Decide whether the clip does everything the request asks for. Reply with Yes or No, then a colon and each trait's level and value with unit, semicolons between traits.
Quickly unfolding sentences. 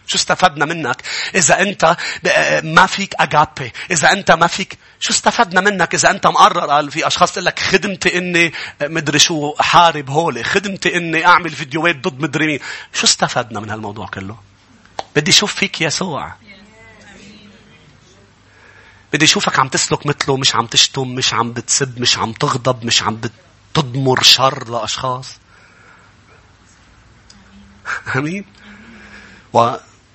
No: slow, 135 wpm